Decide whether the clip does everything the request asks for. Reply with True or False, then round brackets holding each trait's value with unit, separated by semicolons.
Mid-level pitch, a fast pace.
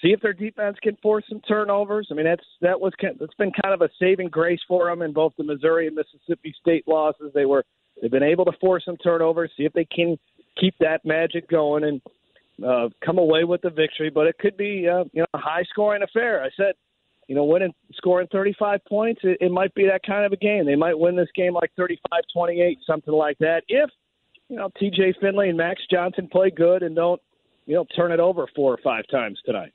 True (175 Hz; 235 wpm)